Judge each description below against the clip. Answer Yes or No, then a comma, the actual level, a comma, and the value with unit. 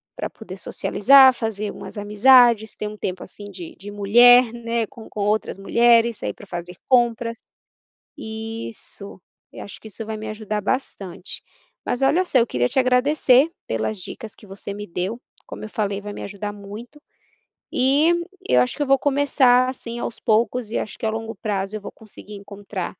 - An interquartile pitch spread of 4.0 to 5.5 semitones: No, average, 3.2 semitones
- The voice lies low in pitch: No, high, 220 Hz